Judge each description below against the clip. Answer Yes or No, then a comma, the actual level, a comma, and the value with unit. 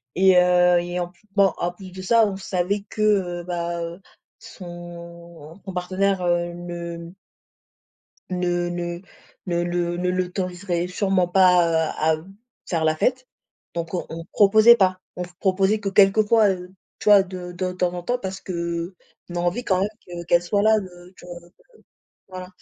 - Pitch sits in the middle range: Yes, medium, 180 Hz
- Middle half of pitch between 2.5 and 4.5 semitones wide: No, narrow, 1.8 semitones